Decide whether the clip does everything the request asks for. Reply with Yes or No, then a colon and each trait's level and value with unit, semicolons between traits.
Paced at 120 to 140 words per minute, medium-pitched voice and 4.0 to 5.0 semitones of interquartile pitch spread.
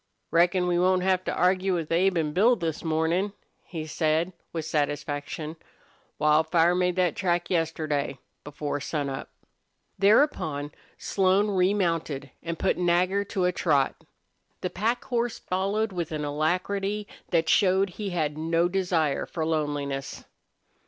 No: slow, 135 wpm; medium, 175 Hz; average, 3.3 semitones